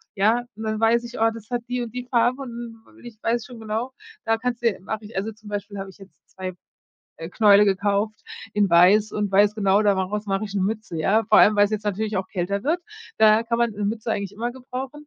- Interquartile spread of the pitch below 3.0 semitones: Yes, narrow, 2.5 semitones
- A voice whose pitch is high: Yes, high, 215 Hz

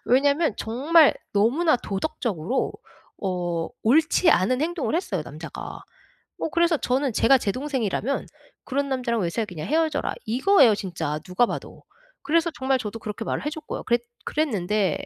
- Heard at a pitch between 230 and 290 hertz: Yes, very high, 250 Hz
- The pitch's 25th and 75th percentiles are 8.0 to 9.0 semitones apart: No, wide, 6.8 semitones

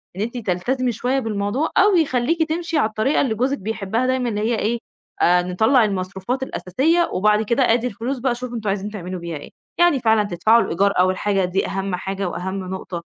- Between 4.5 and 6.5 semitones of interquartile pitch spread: Yes, average, 4.9 semitones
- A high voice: Yes, high, 220 Hz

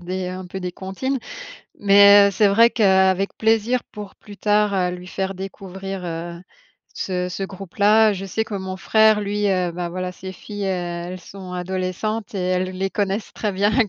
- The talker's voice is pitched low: No, high, 195 Hz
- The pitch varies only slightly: Yes, narrow, 2.1 semitones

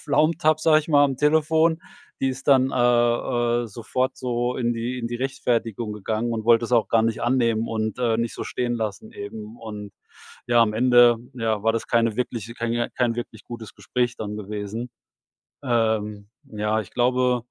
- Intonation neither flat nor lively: No, narrow, 2.2 semitones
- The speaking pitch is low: Yes, low, 120 Hz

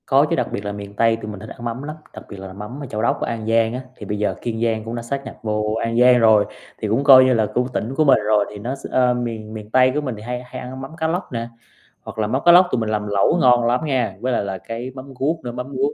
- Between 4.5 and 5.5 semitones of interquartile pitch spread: No, average, 3.2 semitones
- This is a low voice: Yes, low, 115 Hz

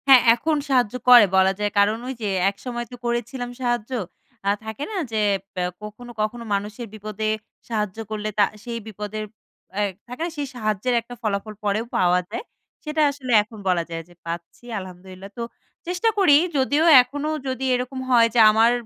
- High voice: Yes, high, 225 Hz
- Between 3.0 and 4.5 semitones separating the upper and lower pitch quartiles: Yes, average, 3.3 semitones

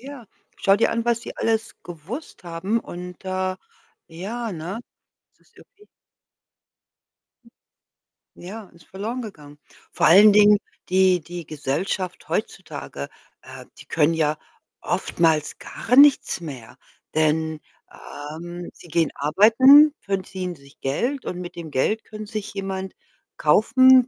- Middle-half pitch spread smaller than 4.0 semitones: No, average, 5.3 semitones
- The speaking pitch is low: No, medium, 185 Hz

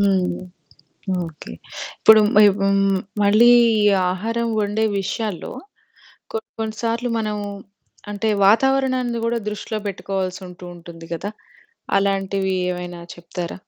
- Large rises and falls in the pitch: No, average, 3.2 semitones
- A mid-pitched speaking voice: No, high, 200 Hz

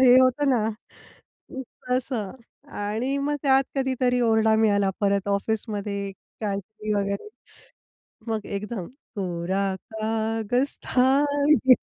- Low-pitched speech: No, high, 220 Hz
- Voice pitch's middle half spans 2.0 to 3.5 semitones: No, average, 4.0 semitones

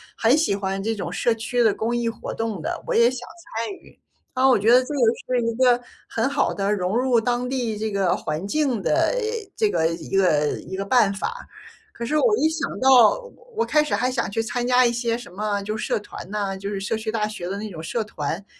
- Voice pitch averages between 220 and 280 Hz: Yes, high, 225 Hz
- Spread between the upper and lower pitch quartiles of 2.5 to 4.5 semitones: Yes, average, 4.0 semitones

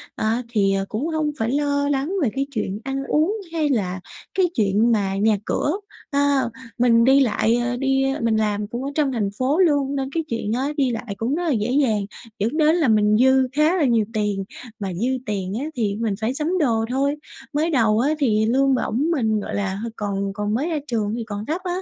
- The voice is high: Yes, high, 245 Hz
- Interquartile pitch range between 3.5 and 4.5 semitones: No, average, 5.0 semitones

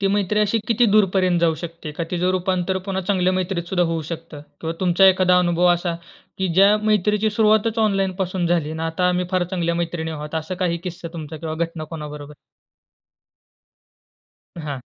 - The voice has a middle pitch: Yes, medium, 180 Hz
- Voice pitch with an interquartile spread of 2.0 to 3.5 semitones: Yes, narrow, 2.6 semitones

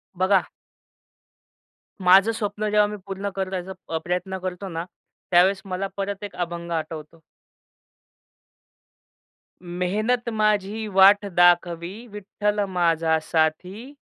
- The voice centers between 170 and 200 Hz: Yes, high, 190 Hz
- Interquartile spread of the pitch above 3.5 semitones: No, average, 2.9 semitones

